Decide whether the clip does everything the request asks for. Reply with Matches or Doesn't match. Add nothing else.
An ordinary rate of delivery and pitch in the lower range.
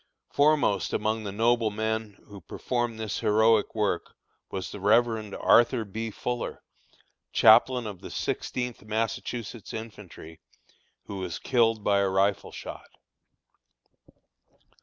Doesn't match